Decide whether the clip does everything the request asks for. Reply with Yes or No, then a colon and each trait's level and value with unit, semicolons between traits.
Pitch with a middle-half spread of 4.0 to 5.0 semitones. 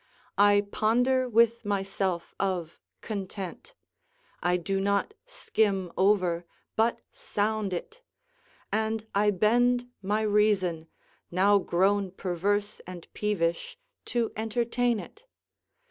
No: average, 2.9 semitones